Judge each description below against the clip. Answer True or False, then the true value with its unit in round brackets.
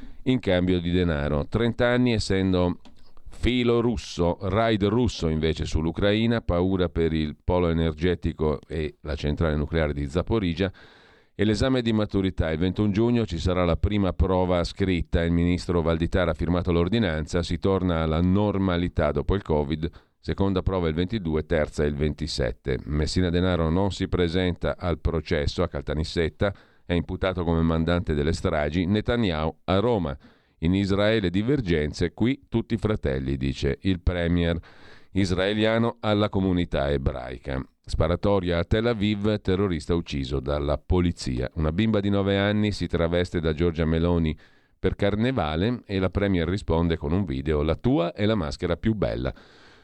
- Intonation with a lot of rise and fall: False (3.6 semitones)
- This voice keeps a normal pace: True (150 wpm)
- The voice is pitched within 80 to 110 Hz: True (90 Hz)